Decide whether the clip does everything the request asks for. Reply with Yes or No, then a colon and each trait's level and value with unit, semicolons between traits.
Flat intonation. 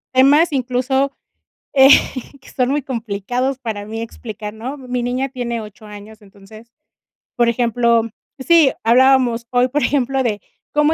No: average, 3.0 semitones